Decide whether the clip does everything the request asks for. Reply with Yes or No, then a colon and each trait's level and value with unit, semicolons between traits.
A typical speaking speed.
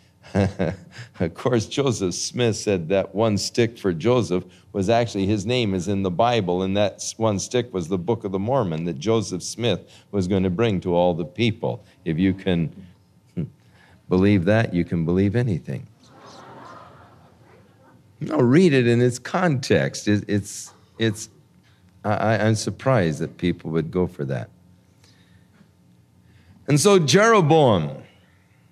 Yes: average, 145 wpm